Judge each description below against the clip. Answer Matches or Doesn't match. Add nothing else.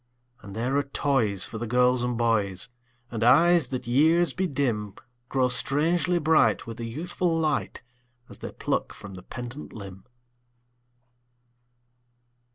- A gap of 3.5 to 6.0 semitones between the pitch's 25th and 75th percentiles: Matches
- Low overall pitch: Matches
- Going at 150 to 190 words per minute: Doesn't match